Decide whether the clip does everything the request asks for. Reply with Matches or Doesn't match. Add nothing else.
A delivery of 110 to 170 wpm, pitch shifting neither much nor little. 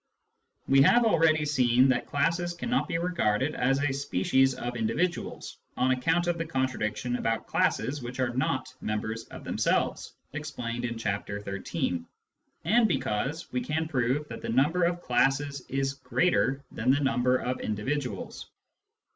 Matches